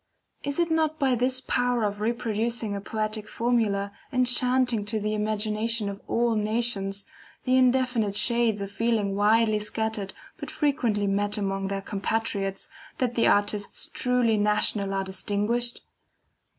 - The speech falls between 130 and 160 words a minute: Yes, average, 140 wpm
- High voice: Yes, high, 220 Hz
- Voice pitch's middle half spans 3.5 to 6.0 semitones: No, average, 2.8 semitones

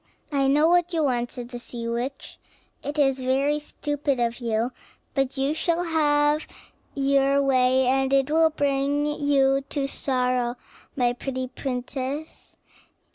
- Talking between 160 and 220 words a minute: No, average, 140 wpm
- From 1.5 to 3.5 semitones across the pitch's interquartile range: Yes, narrow, 2.4 semitones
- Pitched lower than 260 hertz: No, very high, 275 Hz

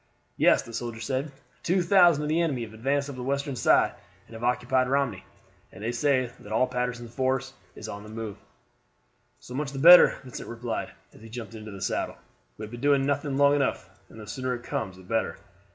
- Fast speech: Yes, fast, 210 wpm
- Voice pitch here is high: No, low, 125 Hz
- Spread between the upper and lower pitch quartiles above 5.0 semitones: No, average, 3.7 semitones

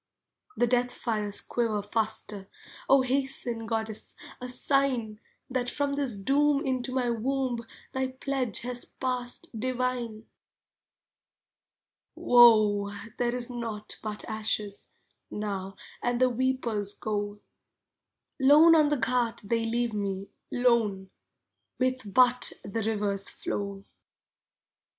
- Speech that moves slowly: Yes, slow, 110 wpm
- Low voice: No, high, 240 Hz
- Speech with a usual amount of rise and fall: Yes, average, 3.3 semitones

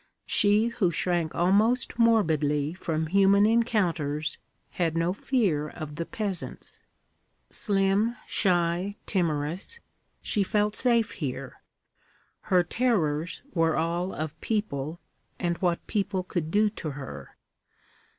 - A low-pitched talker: No, medium, 180 Hz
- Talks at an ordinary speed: No, slow, 110 wpm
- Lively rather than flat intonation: No, average, 4.7 semitones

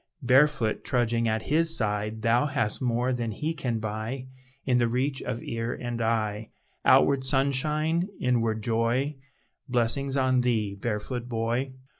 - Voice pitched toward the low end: Yes, low, 120 Hz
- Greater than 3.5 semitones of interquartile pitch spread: No, average, 2.9 semitones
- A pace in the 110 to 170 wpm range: Yes, average, 140 wpm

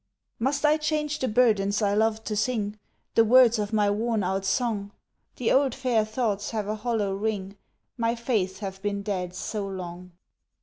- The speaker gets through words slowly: No, average, 175 wpm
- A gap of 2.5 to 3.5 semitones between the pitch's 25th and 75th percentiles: Yes, average, 2.9 semitones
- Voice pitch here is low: No, high, 215 Hz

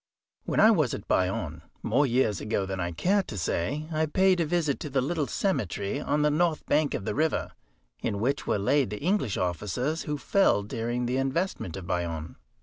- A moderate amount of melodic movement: No, wide, 7.8 semitones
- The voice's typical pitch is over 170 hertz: No, low, 135 Hz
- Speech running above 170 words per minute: Yes, average, 200 wpm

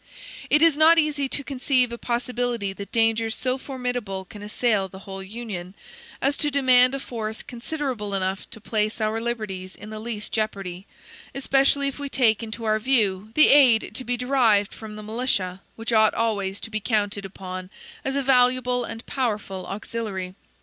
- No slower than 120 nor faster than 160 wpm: No, average, 175 wpm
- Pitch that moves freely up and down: No, average, 3.8 semitones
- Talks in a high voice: Yes, high, 225 Hz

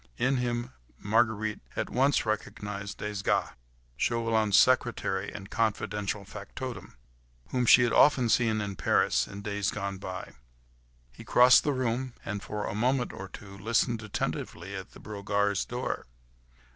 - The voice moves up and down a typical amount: Yes, average, 3.2 semitones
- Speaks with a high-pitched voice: No, low, 105 Hz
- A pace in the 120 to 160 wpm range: Yes, average, 145 wpm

